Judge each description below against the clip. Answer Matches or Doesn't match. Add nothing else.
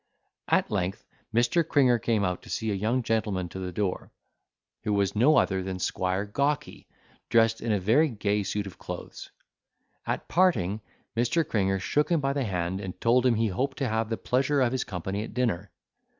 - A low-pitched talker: Matches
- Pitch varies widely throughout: Doesn't match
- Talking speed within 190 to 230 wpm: Matches